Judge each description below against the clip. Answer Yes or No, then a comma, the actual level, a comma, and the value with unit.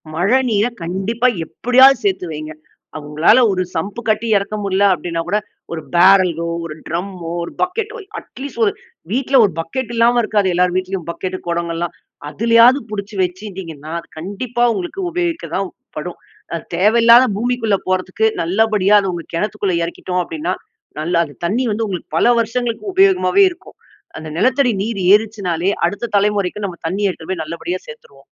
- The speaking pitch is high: Yes, high, 200 Hz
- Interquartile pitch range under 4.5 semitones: No, average, 5.1 semitones